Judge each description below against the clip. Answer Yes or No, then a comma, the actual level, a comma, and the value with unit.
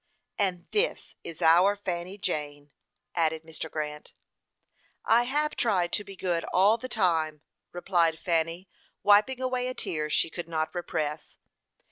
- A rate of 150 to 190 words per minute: No, average, 140 wpm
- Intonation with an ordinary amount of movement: Yes, average, 4.2 semitones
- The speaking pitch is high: No, medium, 175 Hz